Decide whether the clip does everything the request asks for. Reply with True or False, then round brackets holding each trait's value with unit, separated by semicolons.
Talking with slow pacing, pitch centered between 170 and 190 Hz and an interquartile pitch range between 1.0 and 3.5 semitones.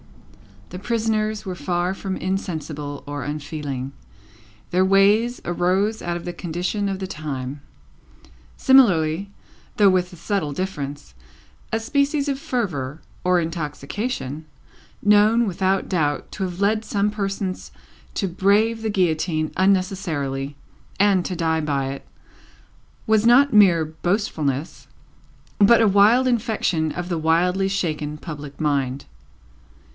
False (125 wpm; 185 Hz; 5.0 semitones)